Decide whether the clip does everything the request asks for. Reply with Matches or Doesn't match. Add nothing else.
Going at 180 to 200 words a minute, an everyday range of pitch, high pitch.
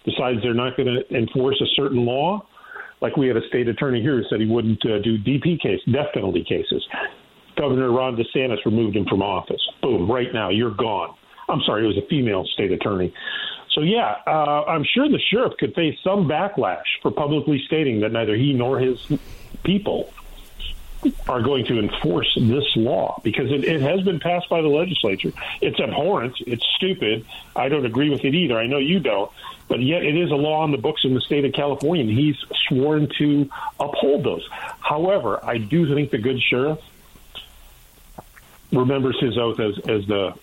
Doesn't match